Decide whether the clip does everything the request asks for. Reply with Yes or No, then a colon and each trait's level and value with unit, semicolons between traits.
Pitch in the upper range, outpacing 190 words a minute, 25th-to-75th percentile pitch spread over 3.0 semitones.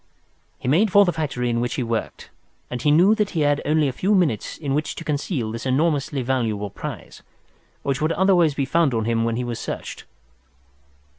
No: medium, 140 Hz; fast, 205 wpm; average, 5.3 semitones